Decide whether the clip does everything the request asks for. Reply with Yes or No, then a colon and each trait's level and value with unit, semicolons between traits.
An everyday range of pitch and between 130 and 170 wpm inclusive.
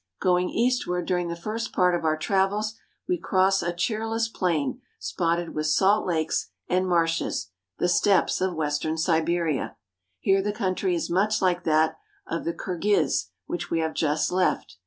Yes: average, 3.1 semitones; average, 160 wpm